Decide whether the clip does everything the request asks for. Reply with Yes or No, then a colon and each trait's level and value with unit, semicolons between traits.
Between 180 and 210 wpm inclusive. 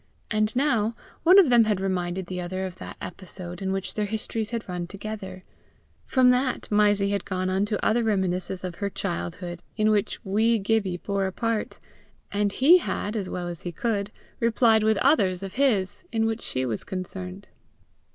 Yes: average, 185 wpm